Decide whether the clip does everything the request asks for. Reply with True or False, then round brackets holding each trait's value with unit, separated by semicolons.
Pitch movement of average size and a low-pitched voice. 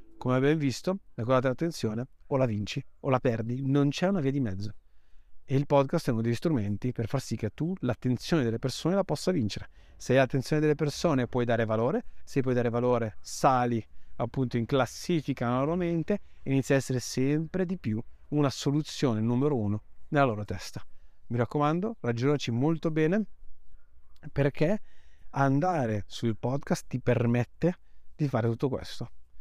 True (4.6 semitones; 130 Hz)